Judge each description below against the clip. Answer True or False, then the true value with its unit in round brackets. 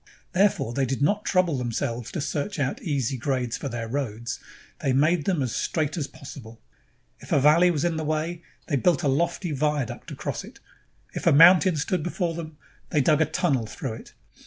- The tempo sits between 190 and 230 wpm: True (200 wpm)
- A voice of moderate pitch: True (150 Hz)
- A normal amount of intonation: True (4.5 semitones)